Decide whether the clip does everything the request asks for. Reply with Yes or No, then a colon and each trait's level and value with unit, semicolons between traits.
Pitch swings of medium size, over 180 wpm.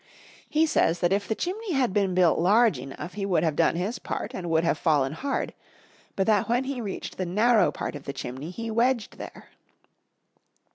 No: wide, 6.0 semitones; average, 200 wpm